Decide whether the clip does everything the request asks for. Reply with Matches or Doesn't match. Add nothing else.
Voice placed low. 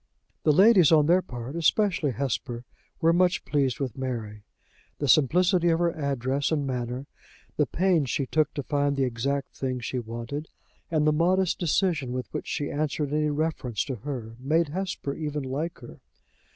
Doesn't match